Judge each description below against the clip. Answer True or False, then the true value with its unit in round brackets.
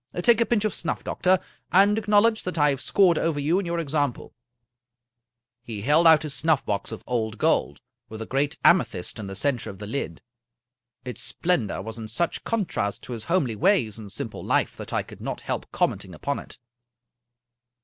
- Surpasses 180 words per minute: True (190 wpm)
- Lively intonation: True (8.3 semitones)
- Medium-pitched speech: True (145 Hz)